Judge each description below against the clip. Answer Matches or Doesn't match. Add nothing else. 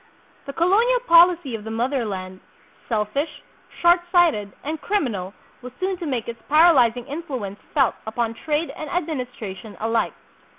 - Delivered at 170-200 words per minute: Doesn't match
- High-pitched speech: Matches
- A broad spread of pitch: Matches